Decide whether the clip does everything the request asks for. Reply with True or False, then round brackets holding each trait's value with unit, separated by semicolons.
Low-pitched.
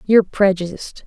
False (195 Hz)